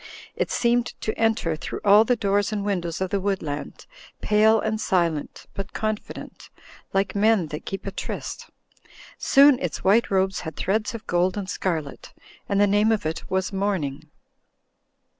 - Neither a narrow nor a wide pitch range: Yes, average, 3.2 semitones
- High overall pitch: Yes, high, 200 Hz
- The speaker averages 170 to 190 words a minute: No, average, 160 wpm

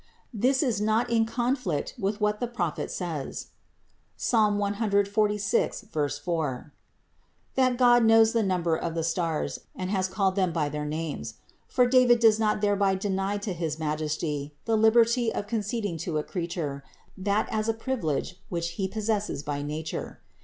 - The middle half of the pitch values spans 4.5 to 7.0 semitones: Yes, average, 5.3 semitones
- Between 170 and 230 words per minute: No, average, 160 wpm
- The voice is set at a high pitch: Yes, high, 200 Hz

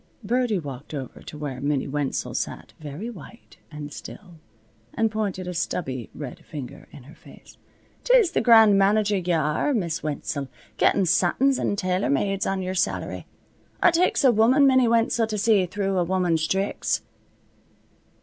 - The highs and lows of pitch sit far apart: Yes, wide, 6.3 semitones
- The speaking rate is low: No, average, 160 wpm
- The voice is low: No, medium, 185 Hz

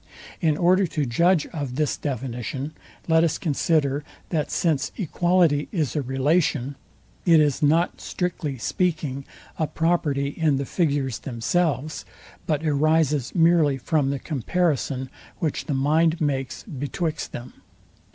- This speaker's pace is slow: Yes, slow, 130 wpm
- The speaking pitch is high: No, medium, 150 Hz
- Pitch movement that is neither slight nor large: Yes, average, 3.3 semitones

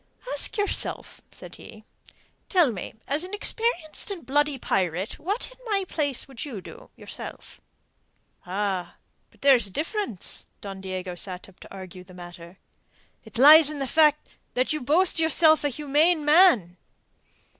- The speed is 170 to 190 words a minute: No, average, 155 wpm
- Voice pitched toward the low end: No, very high, 280 Hz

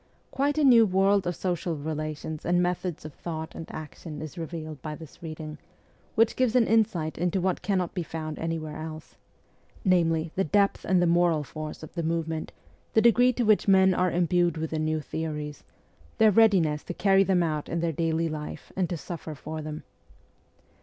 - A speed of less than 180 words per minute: No, average, 185 wpm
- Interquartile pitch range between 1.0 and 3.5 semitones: Yes, average, 3.2 semitones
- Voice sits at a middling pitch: Yes, medium, 165 Hz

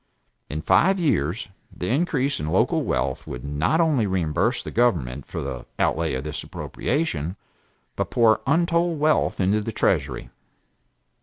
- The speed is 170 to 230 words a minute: No, average, 145 wpm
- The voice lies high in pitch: No, low, 105 Hz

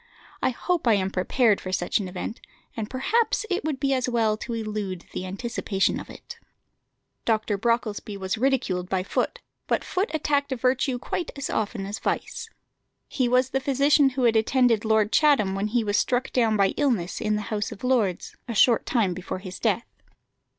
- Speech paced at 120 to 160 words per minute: No, average, 185 wpm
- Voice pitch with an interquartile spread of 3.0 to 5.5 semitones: Yes, average, 4.5 semitones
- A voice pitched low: No, high, 230 Hz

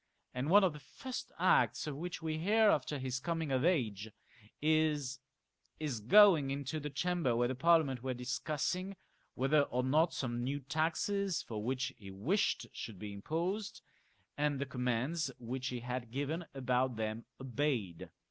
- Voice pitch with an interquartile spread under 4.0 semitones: No, average, 4.5 semitones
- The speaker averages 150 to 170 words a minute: Yes, average, 165 wpm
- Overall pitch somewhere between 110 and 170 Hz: Yes, medium, 140 Hz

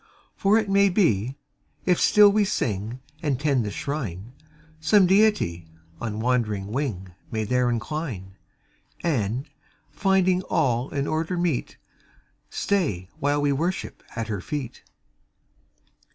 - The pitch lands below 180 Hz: Yes, low, 135 Hz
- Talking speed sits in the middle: No, slow, 125 wpm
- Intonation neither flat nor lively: No, wide, 8.3 semitones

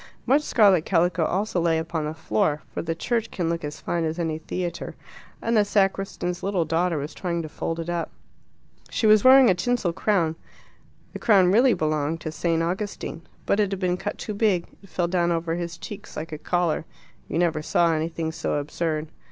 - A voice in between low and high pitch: Yes, medium, 170 Hz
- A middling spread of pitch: Yes, average, 3.3 semitones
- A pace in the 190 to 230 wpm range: Yes, average, 200 wpm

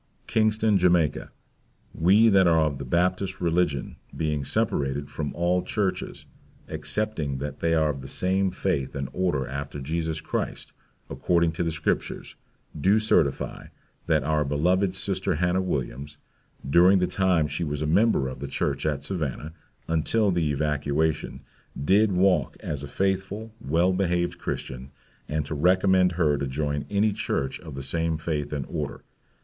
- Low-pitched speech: Yes, very low, 80 Hz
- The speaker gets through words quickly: No, average, 155 wpm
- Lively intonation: No, average, 4.3 semitones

